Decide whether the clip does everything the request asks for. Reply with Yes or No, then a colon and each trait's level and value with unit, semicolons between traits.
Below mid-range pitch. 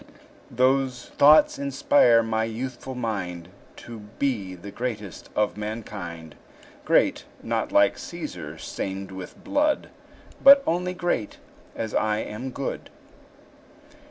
Yes: low, 115 Hz